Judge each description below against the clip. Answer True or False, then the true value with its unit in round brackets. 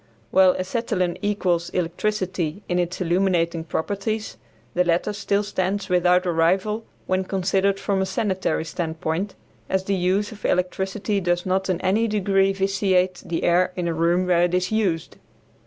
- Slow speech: False (155 wpm)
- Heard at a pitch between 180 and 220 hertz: True (185 Hz)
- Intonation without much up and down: True (1.9 semitones)